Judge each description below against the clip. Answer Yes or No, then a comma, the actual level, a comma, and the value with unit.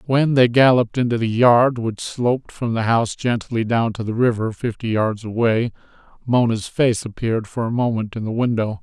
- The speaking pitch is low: Yes, low, 115 Hz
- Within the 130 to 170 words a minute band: No, average, 190 wpm